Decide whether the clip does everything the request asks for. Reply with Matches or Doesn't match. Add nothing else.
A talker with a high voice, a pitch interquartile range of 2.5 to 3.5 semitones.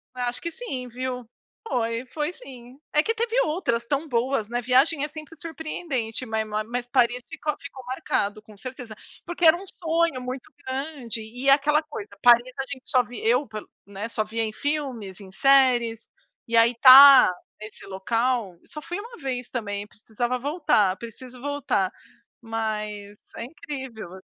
Doesn't match